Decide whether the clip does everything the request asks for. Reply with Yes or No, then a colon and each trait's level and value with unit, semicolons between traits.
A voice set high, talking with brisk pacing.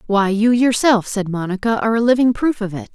Yes: high, 220 Hz; fast, 225 wpm